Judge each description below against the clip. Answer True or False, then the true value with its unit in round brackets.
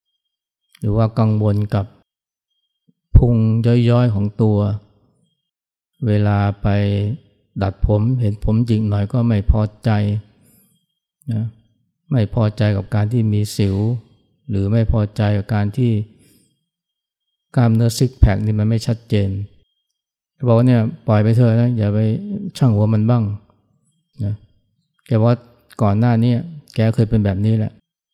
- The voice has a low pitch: True (110 Hz)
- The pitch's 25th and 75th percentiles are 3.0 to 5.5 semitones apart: False (2.6 semitones)